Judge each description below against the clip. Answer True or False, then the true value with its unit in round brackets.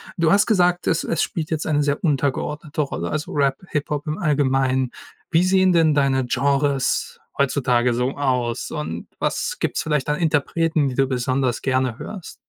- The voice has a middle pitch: True (145 Hz)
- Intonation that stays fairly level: False (3.3 semitones)